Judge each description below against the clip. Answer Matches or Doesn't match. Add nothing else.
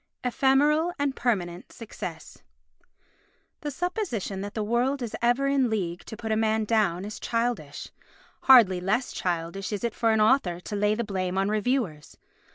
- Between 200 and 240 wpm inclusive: Doesn't match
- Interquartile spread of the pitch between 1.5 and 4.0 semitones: Doesn't match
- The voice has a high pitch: Matches